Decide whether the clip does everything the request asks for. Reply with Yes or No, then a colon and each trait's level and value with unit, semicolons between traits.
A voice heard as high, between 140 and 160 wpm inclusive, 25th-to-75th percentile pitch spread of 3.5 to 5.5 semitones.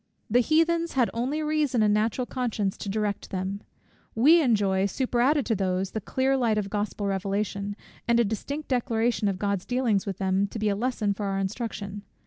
No: high, 215 Hz; average, 185 wpm; average, 4.0 semitones